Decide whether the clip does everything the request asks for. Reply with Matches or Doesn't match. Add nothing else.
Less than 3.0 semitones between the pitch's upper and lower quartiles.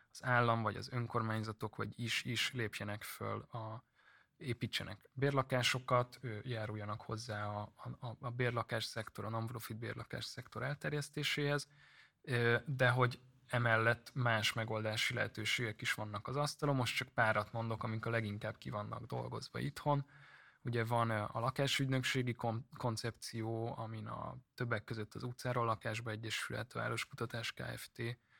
Matches